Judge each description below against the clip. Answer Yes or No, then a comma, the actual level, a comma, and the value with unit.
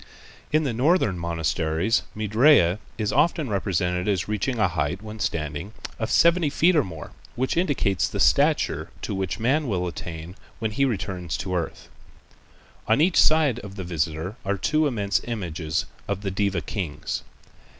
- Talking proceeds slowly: No, average, 160 wpm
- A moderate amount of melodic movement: No, wide, 5.8 semitones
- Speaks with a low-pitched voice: Yes, low, 100 Hz